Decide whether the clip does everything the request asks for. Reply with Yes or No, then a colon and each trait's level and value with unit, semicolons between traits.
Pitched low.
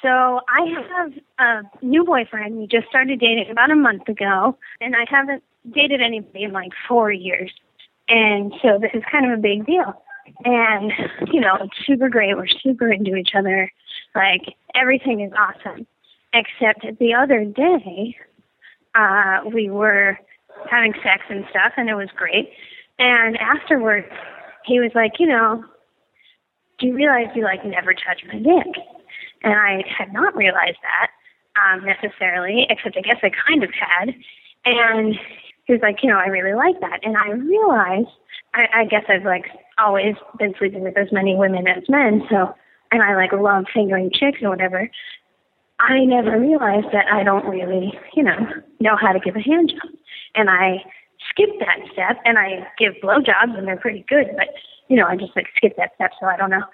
No: high, 220 Hz